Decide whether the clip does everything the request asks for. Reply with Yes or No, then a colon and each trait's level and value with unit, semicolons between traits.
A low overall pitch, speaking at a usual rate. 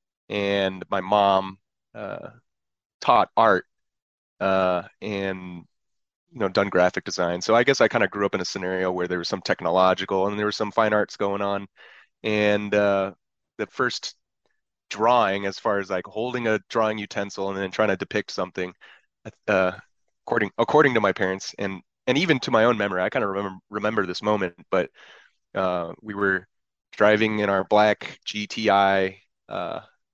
Yes: low, 100 Hz; average, 170 wpm